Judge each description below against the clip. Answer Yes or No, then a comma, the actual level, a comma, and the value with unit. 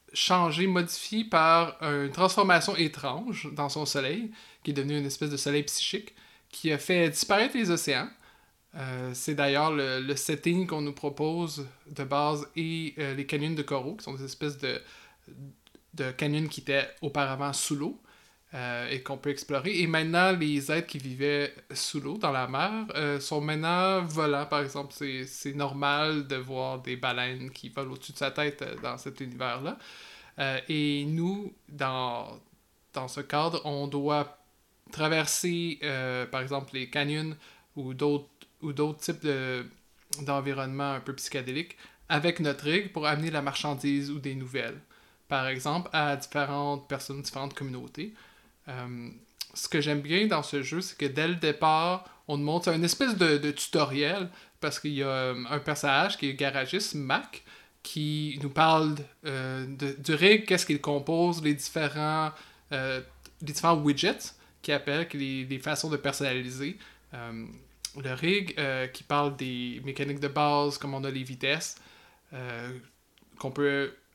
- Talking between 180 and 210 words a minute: No, average, 170 wpm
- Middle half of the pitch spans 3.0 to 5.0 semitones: No, narrow, 2.4 semitones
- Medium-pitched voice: Yes, medium, 145 Hz